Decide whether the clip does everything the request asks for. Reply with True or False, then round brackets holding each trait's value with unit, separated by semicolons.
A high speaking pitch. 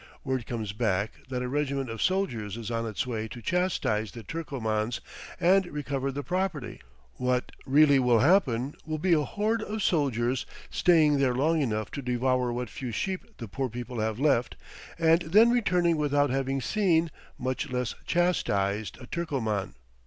False (135 Hz)